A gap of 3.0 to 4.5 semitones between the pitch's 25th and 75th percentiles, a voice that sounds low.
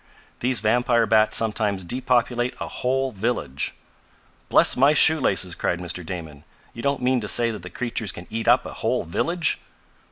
No: average, 5.0 semitones; low, 115 Hz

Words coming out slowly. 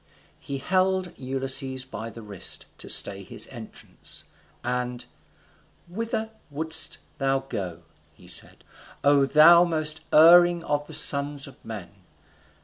Yes: slow, 125 wpm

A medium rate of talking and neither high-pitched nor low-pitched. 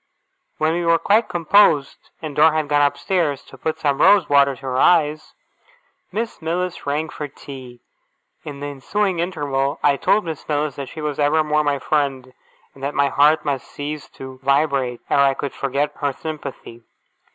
Yes: average, 180 wpm; medium, 145 Hz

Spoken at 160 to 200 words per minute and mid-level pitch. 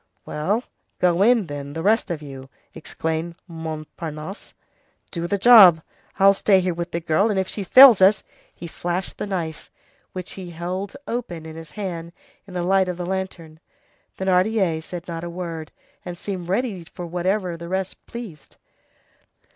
Yes: average, 165 wpm; medium, 180 Hz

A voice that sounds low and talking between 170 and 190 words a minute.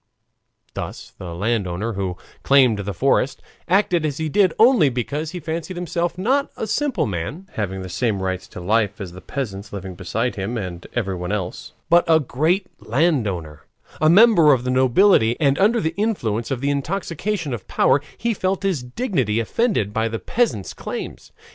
Yes: low, 130 Hz; average, 175 wpm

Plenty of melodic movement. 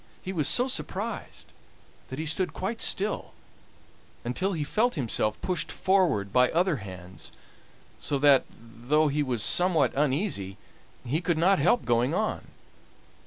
Yes: wide, 7.3 semitones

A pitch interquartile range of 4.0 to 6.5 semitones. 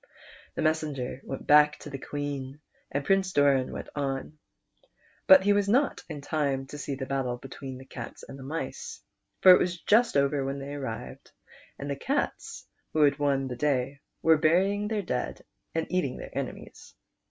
No: average, 3.3 semitones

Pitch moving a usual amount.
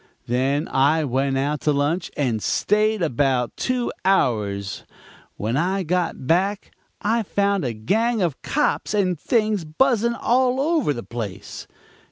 No: wide, 8.1 semitones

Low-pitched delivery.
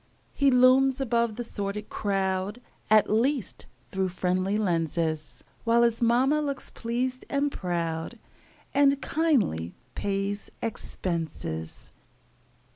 No: high, 215 Hz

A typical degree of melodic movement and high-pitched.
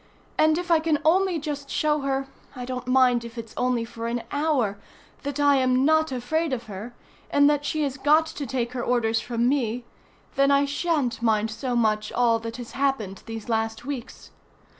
Yes: average, 3.8 semitones; very high, 255 Hz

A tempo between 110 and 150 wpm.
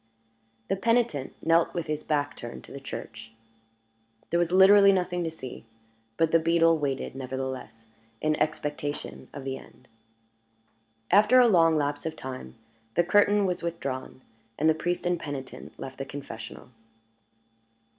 Yes: average, 145 wpm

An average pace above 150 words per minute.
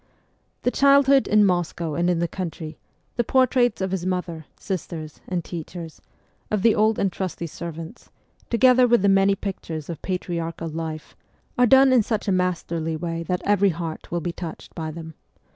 Yes: average, 180 wpm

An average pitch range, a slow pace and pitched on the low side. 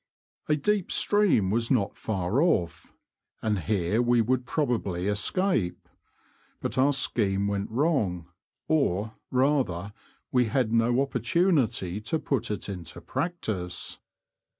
No: wide, 5.9 semitones; slow, 125 wpm; low, 115 Hz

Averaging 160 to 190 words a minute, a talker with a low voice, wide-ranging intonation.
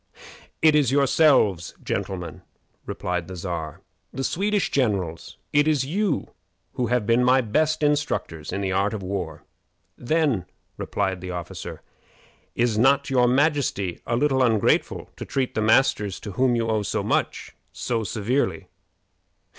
No: average, 145 wpm; low, 120 Hz; wide, 6.5 semitones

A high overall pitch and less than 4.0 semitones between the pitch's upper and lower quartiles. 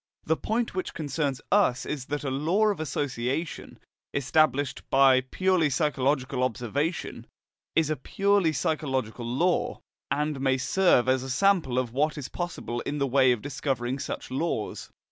No: medium, 140 Hz; average, 3.6 semitones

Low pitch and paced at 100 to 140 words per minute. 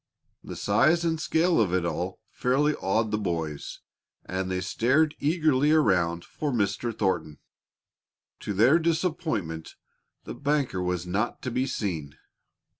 Yes: low, 110 Hz; slow, 135 wpm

